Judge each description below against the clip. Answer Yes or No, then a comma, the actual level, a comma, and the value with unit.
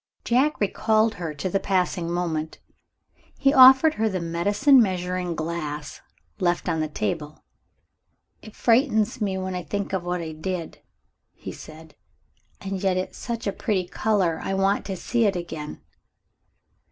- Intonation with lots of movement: No, average, 4.1 semitones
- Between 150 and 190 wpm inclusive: Yes, average, 155 wpm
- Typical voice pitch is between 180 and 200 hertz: Yes, medium, 185 Hz